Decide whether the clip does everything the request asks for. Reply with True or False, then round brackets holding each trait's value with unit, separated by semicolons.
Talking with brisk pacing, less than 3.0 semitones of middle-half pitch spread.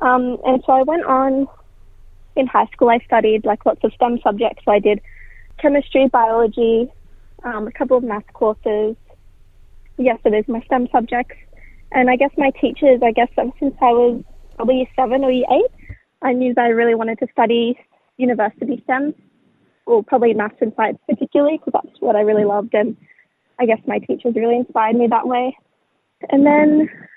False (190 wpm; 2.6 semitones)